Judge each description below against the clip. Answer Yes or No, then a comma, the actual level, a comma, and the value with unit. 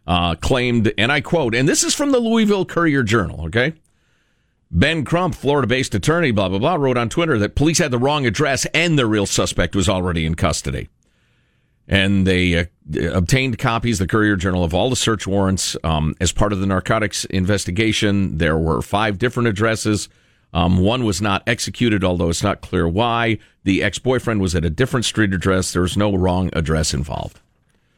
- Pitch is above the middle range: No, low, 105 Hz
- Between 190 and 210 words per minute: Yes, average, 195 wpm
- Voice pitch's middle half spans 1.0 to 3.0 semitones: No, average, 5.3 semitones